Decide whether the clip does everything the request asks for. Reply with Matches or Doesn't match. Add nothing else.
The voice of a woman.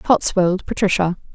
Matches